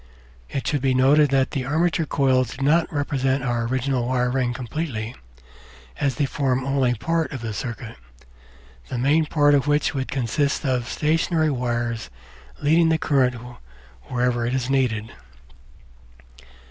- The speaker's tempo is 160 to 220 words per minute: No, average, 145 wpm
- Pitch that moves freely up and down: No, average, 2.9 semitones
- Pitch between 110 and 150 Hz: Yes, low, 135 Hz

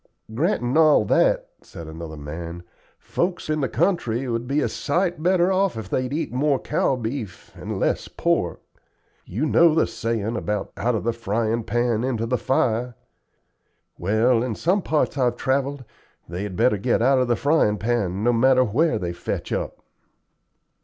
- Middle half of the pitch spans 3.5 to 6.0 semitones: Yes, average, 4.6 semitones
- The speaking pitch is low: Yes, low, 120 Hz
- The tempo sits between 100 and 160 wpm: No, average, 170 wpm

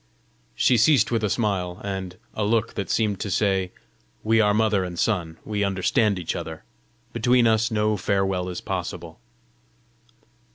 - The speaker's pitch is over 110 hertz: No, low, 100 Hz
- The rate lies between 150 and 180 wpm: Yes, average, 155 wpm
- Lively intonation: No, average, 3.1 semitones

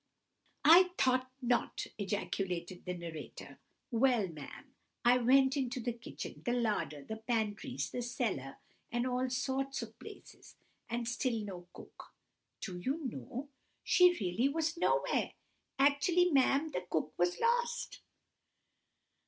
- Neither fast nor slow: No, slow, 130 wpm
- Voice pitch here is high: Yes, high, 245 Hz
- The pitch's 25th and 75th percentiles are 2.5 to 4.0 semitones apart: No, wide, 5.5 semitones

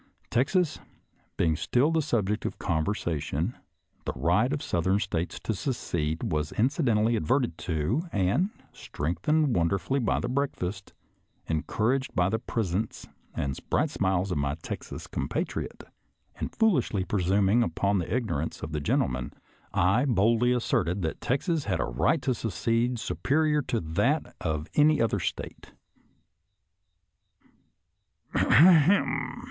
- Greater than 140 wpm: No, slow, 135 wpm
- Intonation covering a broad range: Yes, wide, 7.4 semitones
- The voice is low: Yes, low, 105 Hz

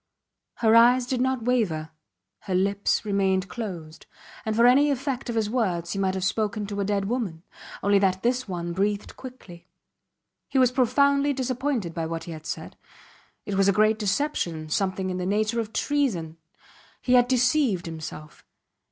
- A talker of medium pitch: No, high, 210 Hz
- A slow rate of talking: No, average, 170 wpm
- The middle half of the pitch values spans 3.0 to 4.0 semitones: No, average, 5.2 semitones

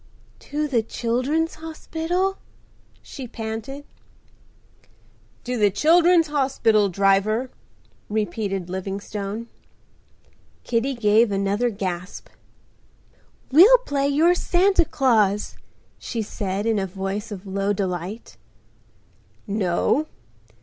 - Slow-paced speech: Yes, slow, 90 wpm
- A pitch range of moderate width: No, wide, 6.4 semitones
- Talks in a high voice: Yes, high, 225 Hz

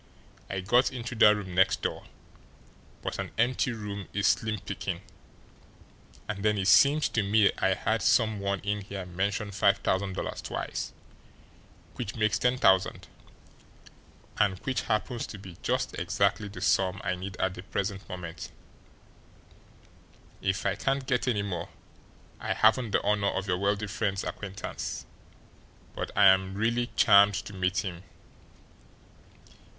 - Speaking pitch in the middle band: No, low, 100 Hz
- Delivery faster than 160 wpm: No, average, 145 wpm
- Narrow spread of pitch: Yes, narrow, 2.3 semitones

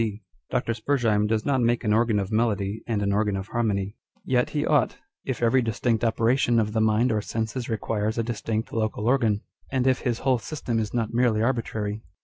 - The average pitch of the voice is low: Yes, low, 115 Hz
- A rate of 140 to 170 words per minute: No, fast, 205 wpm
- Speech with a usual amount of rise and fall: No, narrow, 2.1 semitones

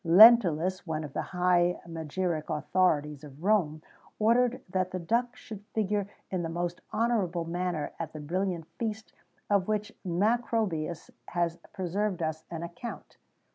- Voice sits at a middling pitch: Yes, medium, 180 Hz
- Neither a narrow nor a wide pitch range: Yes, average, 4.1 semitones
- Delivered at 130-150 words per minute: Yes, average, 140 wpm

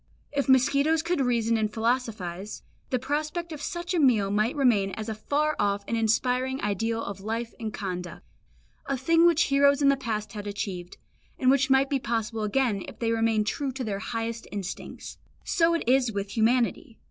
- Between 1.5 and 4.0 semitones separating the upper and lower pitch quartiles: No, average, 4.5 semitones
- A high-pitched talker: Yes, high, 235 Hz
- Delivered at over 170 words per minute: Yes, average, 185 wpm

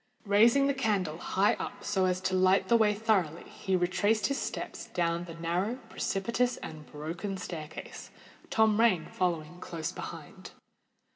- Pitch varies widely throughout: No, average, 4.2 semitones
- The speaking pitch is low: No, medium, 185 Hz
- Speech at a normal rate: Yes, average, 150 wpm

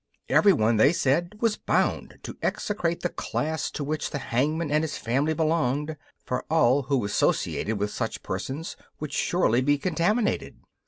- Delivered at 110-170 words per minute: Yes, average, 155 wpm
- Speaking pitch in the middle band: Yes, medium, 150 Hz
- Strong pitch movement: No, average, 4.4 semitones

